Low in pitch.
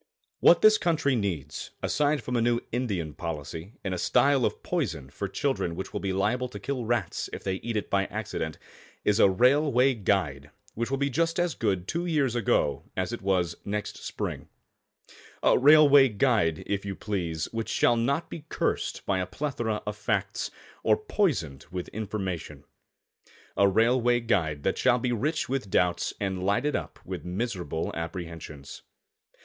Yes: low, 105 Hz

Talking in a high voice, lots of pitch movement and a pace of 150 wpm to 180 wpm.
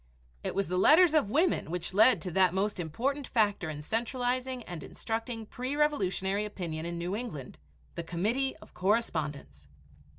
Yes: high, 205 Hz; wide, 6.4 semitones; average, 160 wpm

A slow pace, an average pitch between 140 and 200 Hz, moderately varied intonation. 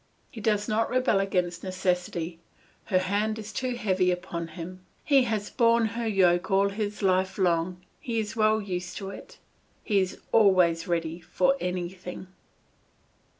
No: average, 150 wpm; high, 190 Hz; average, 3.3 semitones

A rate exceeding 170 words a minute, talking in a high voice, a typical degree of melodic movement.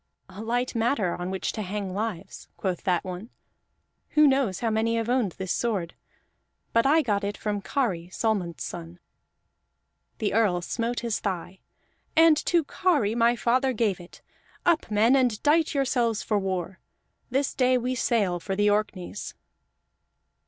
No: average, 155 wpm; high, 220 Hz; average, 4.6 semitones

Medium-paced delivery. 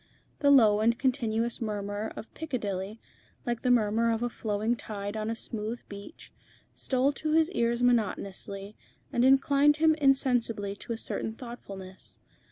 Yes: average, 150 wpm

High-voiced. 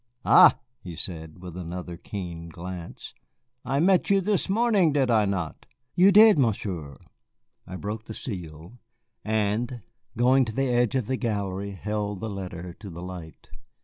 No: low, 105 Hz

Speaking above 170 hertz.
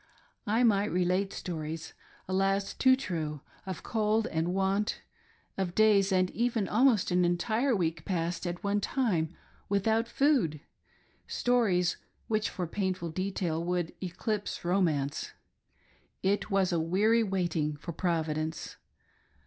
Yes: high, 190 Hz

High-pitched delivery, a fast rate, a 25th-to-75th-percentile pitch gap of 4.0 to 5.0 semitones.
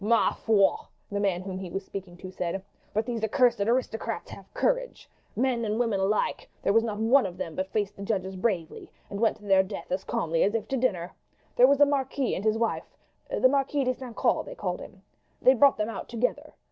Yes: high, 220 Hz; fast, 225 wpm; average, 4.5 semitones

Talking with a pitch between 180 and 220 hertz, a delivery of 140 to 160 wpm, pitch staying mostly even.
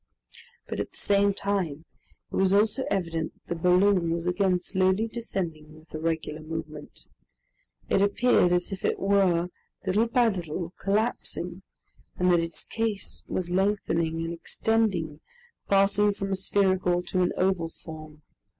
No: medium, 185 Hz; average, 150 wpm; average, 3.2 semitones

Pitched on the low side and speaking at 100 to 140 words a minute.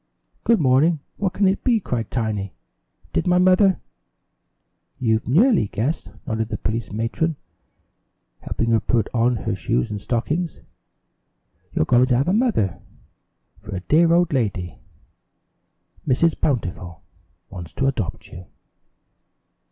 Yes: low, 125 Hz; slow, 135 wpm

